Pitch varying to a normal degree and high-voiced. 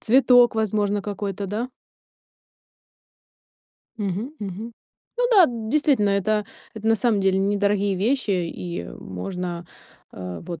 Yes: average, 3.0 semitones; high, 205 Hz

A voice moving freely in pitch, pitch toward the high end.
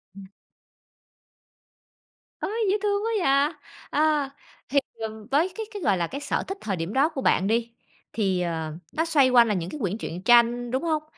Yes: wide, 7.3 semitones; high, 245 Hz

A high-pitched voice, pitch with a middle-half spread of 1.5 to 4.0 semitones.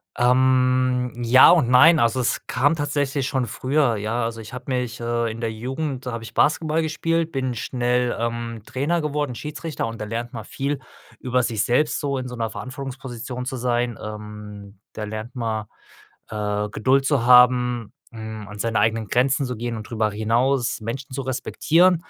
No: low, 125 Hz; average, 2.9 semitones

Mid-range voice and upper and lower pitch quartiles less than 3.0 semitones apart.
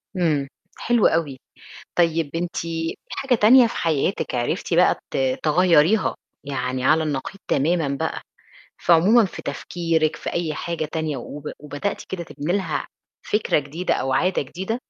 No: medium, 165 Hz; average, 3.8 semitones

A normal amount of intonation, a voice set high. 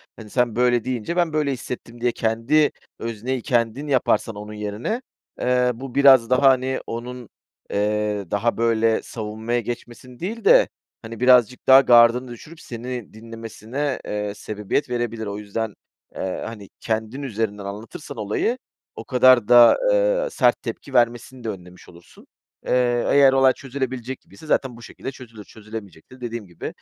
No: average, 3.0 semitones; low, 120 Hz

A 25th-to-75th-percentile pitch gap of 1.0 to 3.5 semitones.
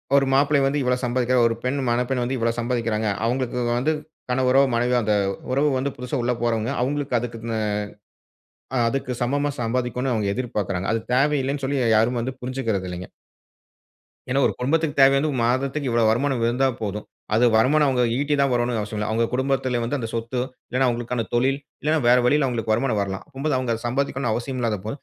Yes: average, 2.8 semitones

